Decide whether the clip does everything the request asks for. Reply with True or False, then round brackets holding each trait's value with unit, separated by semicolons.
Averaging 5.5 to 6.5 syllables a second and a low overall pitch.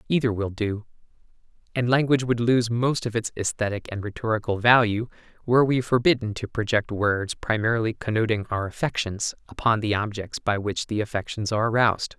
True (5.7 syllables/s; 110 Hz)